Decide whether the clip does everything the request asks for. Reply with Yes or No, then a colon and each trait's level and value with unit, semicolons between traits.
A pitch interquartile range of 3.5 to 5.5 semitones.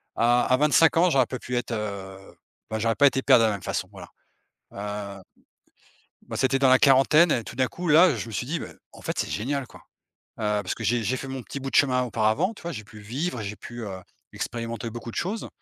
Yes: average, 4.2 semitones